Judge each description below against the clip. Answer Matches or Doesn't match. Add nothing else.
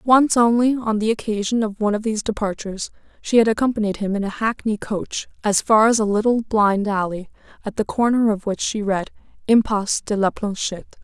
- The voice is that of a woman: Matches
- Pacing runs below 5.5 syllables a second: Doesn't match